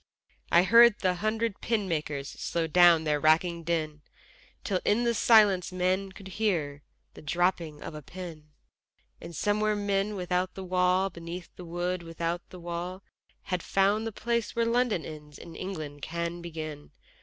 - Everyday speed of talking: Yes, average, 160 wpm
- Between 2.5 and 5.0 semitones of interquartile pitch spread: Yes, average, 3.1 semitones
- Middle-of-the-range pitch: Yes, medium, 180 Hz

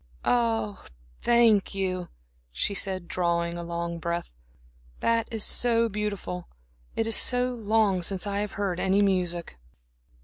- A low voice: No, high, 195 Hz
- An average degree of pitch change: Yes, average, 4.2 semitones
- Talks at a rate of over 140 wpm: No, slow, 135 wpm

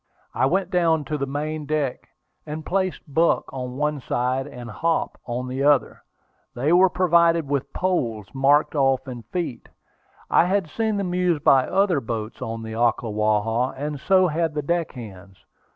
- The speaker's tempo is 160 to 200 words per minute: Yes, average, 170 wpm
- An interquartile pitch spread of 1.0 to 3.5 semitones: No, average, 5.3 semitones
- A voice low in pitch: No, medium, 145 Hz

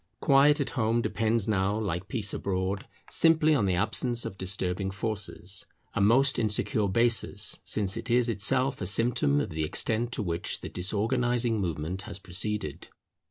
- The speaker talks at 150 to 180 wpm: Yes, average, 160 wpm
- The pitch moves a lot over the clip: No, average, 3.8 semitones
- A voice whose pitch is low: Yes, low, 105 Hz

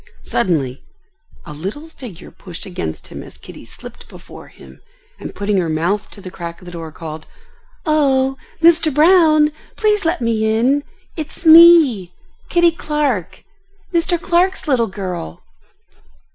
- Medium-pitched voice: No, high, 235 Hz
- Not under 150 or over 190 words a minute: No, average, 140 wpm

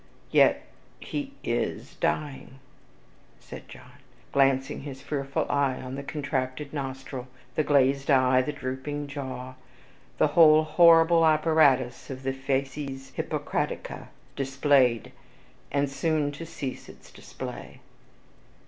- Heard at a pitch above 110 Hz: Yes, medium, 140 Hz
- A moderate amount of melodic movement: No, narrow, 2.1 semitones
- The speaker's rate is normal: No, slow, 110 wpm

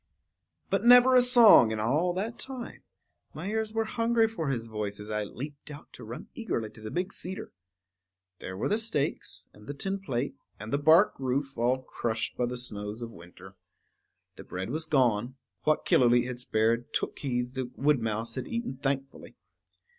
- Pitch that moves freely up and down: Yes, wide, 8.7 semitones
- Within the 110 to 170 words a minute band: No, average, 180 wpm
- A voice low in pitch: Yes, low, 130 Hz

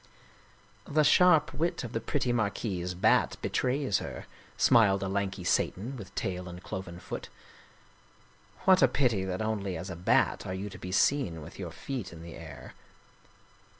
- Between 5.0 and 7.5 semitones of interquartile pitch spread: Yes, wide, 5.5 semitones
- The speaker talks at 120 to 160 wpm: No, average, 175 wpm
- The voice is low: Yes, low, 100 Hz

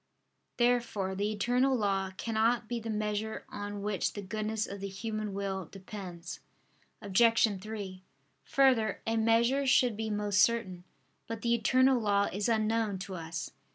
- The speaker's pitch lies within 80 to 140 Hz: No, high, 215 Hz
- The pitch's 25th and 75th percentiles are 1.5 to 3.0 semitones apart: Yes, narrow, 2.5 semitones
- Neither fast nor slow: Yes, average, 150 wpm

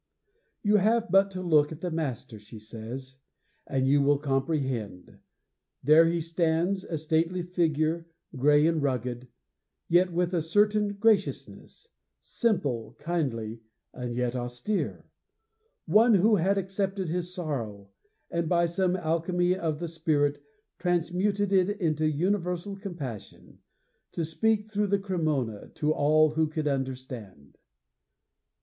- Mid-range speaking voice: Yes, medium, 165 Hz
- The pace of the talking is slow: Yes, slow, 130 wpm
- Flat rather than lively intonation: No, average, 5.2 semitones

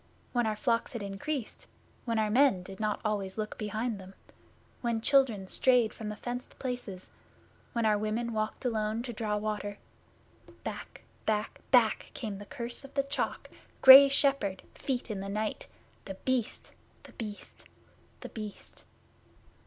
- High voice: Yes, high, 220 Hz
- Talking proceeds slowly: No, average, 155 wpm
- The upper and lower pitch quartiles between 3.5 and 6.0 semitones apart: No, average, 2.9 semitones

